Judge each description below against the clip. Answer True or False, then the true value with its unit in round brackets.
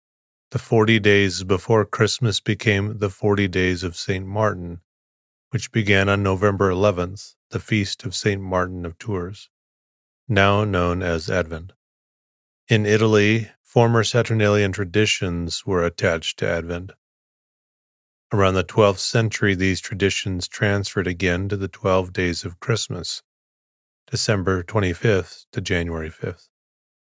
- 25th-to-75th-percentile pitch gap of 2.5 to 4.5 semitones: True (2.8 semitones)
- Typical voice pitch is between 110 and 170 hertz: False (100 Hz)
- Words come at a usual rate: False (125 wpm)